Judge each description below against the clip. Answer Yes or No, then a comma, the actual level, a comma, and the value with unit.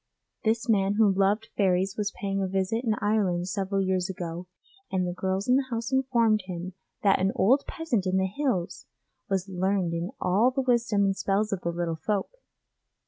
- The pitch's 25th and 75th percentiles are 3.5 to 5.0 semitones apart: No, average, 2.9 semitones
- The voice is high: Yes, high, 195 Hz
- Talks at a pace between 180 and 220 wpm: Yes, average, 190 wpm